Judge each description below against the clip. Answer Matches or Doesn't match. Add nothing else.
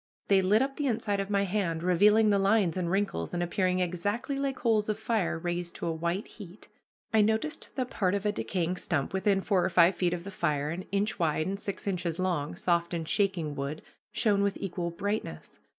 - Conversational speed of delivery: Doesn't match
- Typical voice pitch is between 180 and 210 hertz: Matches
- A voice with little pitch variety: Doesn't match